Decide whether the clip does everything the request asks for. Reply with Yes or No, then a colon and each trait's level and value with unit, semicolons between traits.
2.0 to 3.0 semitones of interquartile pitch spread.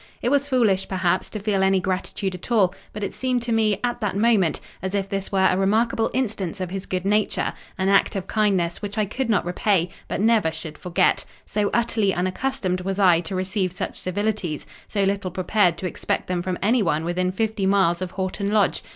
Yes: average, 2.7 semitones